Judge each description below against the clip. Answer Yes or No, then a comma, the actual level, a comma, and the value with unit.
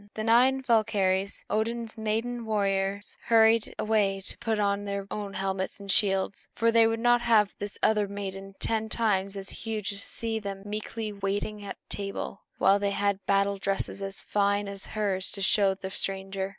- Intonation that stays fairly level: Yes, narrow, 2.0 semitones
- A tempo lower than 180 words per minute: Yes, average, 170 wpm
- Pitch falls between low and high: No, high, 205 Hz